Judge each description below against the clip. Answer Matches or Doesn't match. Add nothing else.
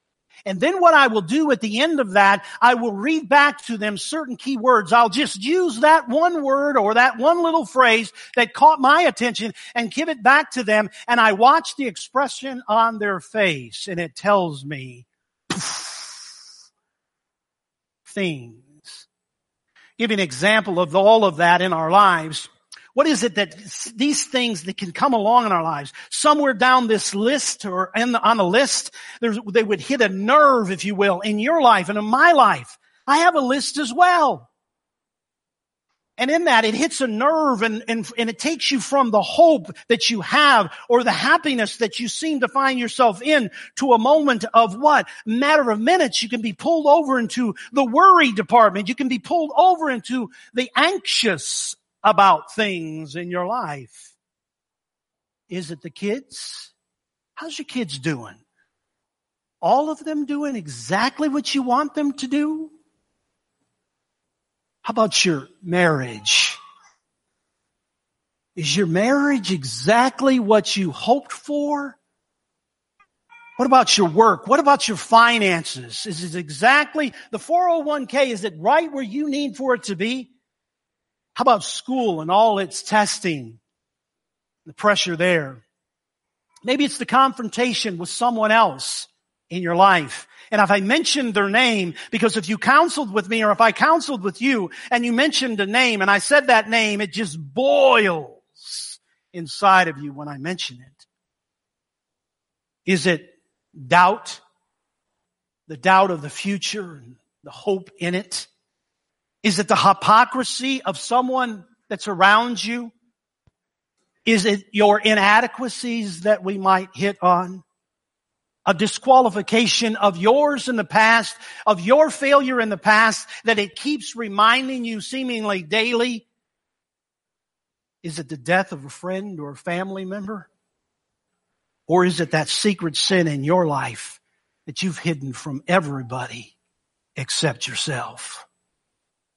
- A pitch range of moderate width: Doesn't match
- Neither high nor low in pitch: Doesn't match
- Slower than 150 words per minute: Doesn't match